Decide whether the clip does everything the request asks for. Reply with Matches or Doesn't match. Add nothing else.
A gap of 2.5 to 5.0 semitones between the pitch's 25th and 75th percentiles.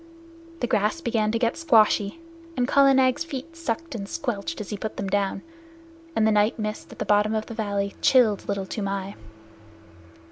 Matches